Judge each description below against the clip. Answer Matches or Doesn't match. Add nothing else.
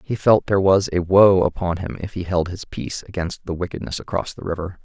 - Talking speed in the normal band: Doesn't match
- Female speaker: Doesn't match